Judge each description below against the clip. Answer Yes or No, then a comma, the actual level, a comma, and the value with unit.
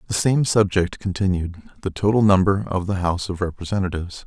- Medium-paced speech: Yes, average, 170 wpm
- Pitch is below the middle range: Yes, very low, 95 Hz